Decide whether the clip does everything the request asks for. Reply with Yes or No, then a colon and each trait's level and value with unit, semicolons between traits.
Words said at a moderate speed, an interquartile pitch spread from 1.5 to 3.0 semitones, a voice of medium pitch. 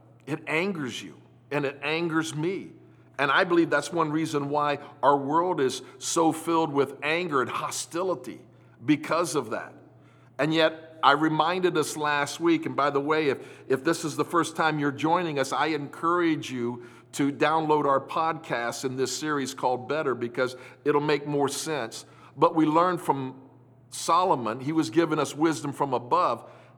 Yes: average, 170 wpm; average, 2.7 semitones; medium, 150 Hz